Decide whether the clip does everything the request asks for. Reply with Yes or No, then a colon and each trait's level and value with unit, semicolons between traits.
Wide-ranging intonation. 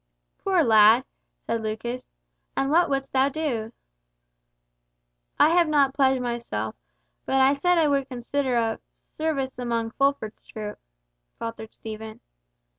No: average, 3.9 semitones